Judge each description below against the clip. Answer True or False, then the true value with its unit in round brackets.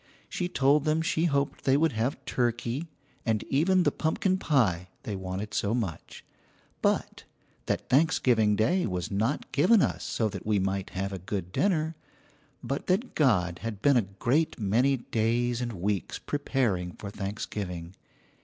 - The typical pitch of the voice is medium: False (115 Hz)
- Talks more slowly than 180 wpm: True (155 wpm)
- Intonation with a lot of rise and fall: True (6.5 semitones)